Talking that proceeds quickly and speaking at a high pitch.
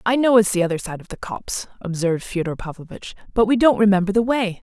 Yes: fast, 230 wpm; high, 200 Hz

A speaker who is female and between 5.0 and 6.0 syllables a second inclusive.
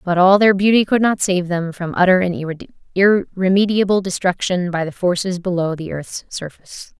Yes: female; 5.8 syllables/s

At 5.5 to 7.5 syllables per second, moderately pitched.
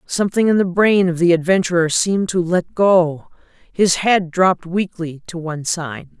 No: 4.8 syllables/s; medium, 175 Hz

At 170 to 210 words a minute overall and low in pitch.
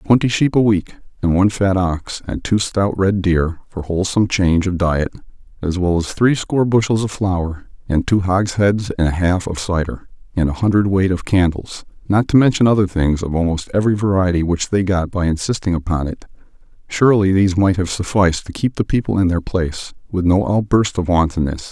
Yes: average, 195 wpm; very low, 95 Hz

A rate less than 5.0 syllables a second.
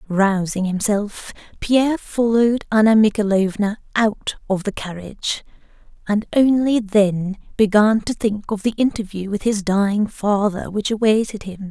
Yes: 4.4 syllables/s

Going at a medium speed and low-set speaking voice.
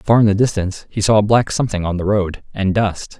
No: fast, 265 wpm; low, 100 Hz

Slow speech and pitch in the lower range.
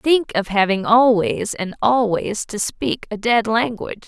No: slow, 130 wpm; high, 220 Hz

